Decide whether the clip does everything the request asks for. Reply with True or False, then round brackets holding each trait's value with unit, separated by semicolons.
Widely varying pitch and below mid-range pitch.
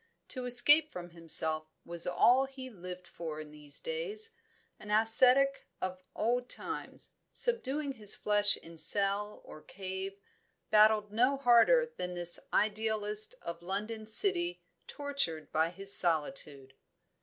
False (6.8 semitones; 210 Hz)